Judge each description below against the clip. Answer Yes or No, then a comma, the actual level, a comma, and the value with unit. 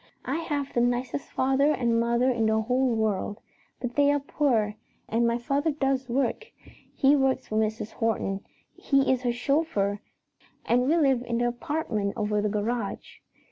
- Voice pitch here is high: Yes, high, 245 Hz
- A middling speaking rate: Yes, average, 170 wpm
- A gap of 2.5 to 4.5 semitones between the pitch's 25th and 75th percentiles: Yes, average, 3.8 semitones